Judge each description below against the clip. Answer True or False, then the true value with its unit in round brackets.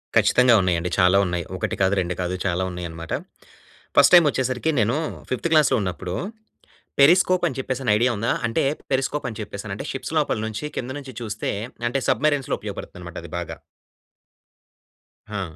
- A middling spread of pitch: False (6.9 semitones)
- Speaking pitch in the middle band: False (115 Hz)